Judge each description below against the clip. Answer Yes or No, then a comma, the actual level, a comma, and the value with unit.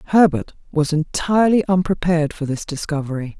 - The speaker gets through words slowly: Yes, slow, 125 wpm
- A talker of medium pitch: Yes, medium, 165 Hz